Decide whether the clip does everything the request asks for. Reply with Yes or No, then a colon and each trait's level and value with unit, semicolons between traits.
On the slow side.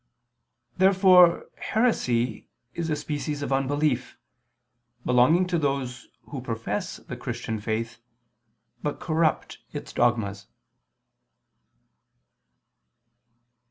Yes: slow, 85 wpm